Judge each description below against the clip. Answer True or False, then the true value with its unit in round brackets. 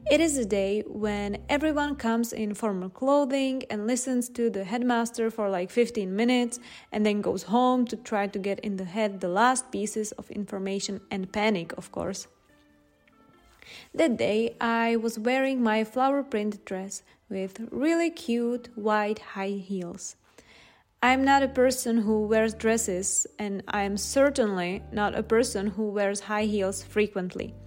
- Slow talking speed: False (160 wpm)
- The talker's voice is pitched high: True (215 Hz)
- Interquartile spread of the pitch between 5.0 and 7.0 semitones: False (3.4 semitones)